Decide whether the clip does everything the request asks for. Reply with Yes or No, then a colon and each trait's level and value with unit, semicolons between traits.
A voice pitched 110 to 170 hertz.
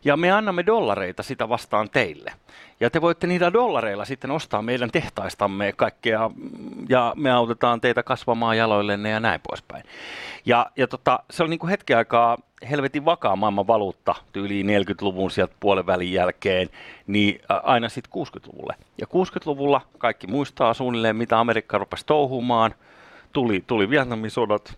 Yes: low, 120 Hz